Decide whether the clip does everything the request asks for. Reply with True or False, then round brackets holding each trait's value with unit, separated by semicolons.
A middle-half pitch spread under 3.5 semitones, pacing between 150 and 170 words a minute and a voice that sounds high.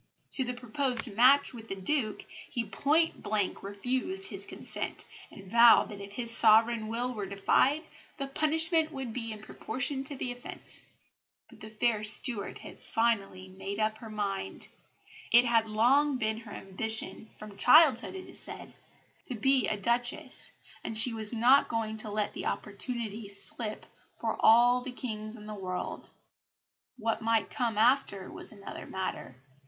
True (2.9 semitones; 160 wpm; 225 Hz)